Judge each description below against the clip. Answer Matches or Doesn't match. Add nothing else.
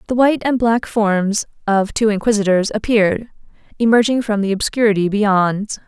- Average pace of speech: Matches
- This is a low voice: Doesn't match